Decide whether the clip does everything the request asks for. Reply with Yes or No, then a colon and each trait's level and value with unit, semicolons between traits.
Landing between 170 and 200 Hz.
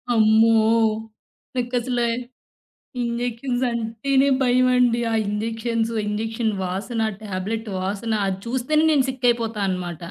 No: high, 230 Hz